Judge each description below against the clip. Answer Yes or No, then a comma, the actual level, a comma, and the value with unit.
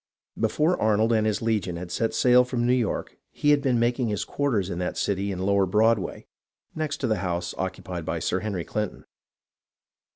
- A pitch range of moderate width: Yes, average, 4.3 semitones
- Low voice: Yes, low, 110 Hz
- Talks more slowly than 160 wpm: No, average, 200 wpm